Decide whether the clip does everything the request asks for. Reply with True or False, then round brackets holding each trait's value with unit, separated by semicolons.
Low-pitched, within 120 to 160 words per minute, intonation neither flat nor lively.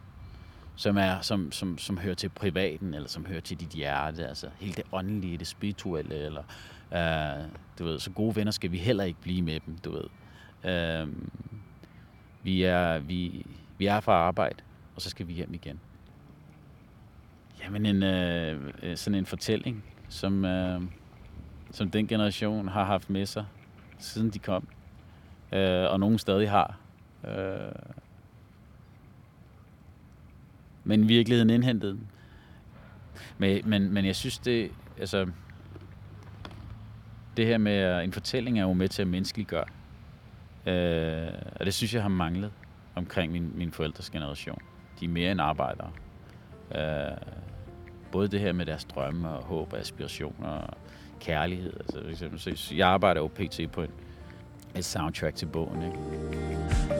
True (95 Hz; 145 wpm; 3.3 semitones)